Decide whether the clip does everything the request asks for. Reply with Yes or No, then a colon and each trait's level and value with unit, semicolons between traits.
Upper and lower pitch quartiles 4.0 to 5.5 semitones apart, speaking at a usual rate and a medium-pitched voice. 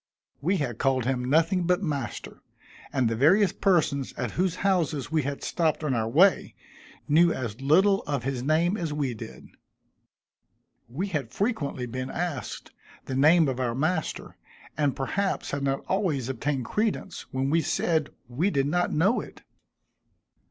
Yes: average, 4.9 semitones; average, 160 wpm; medium, 150 Hz